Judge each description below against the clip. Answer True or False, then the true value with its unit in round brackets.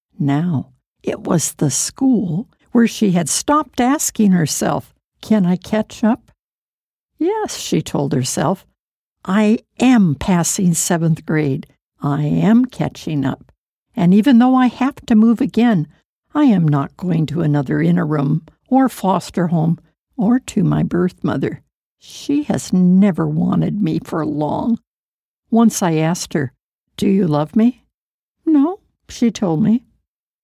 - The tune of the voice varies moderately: False (7.0 semitones)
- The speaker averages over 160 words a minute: False (140 wpm)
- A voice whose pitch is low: False (185 Hz)